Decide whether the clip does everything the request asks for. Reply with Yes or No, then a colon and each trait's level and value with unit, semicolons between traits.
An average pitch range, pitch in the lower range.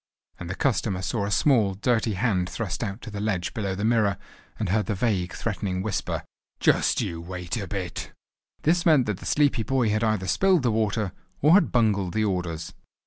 Yes: average, 3.6 semitones; low, 105 Hz